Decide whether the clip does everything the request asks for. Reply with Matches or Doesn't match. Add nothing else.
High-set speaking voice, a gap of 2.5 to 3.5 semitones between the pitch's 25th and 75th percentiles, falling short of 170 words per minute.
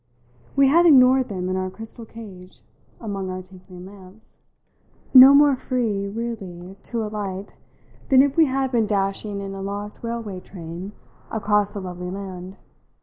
Doesn't match